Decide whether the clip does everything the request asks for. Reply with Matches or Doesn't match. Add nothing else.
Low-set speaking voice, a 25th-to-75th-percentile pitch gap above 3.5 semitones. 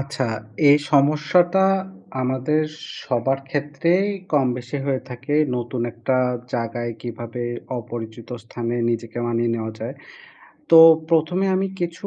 Matches